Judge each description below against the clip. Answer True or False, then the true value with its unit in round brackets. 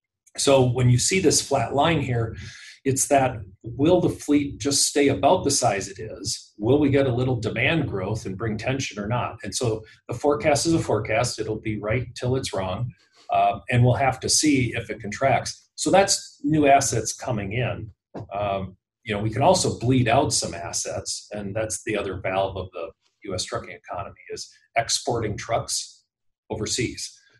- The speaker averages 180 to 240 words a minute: True (185 wpm)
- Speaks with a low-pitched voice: True (125 Hz)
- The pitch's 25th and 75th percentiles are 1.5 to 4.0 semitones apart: False (4.5 semitones)